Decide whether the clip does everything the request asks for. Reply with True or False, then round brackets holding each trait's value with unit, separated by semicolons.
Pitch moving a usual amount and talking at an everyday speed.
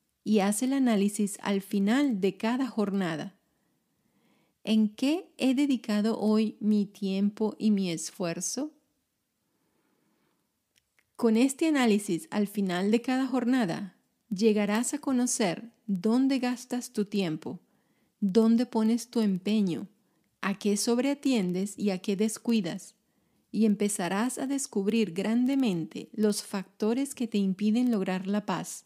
False (3.3 semitones; 120 wpm)